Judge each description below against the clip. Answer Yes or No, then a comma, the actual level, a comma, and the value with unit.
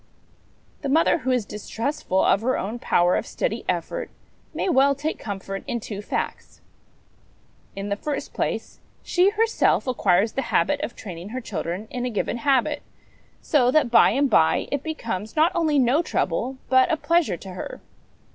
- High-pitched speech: Yes, very high, 250 Hz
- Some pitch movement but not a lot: No, wide, 6.2 semitones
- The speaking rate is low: No, average, 170 wpm